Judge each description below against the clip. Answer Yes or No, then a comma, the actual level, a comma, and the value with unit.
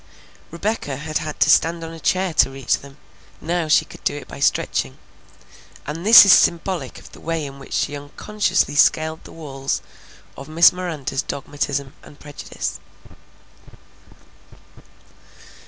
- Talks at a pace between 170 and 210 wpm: No, average, 145 wpm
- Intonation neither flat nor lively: Yes, average, 3.2 semitones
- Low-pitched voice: No, medium, 155 Hz